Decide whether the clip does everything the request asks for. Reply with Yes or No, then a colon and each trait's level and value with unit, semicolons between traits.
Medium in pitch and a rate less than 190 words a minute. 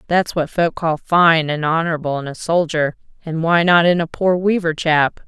No: medium, 165 Hz; fast, 205 wpm